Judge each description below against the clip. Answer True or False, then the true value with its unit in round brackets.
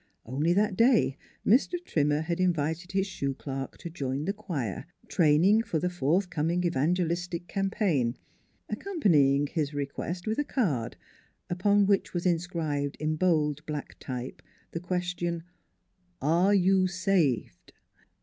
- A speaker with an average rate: False (130 wpm)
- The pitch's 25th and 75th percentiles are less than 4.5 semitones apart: True (4.0 semitones)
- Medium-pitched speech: True (170 Hz)